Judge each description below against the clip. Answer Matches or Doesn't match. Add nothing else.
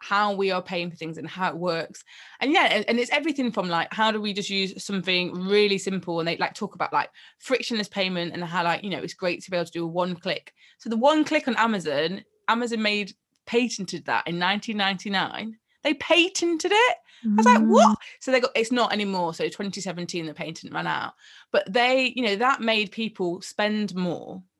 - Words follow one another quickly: Matches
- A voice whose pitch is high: Matches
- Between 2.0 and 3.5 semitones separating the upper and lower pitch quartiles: Doesn't match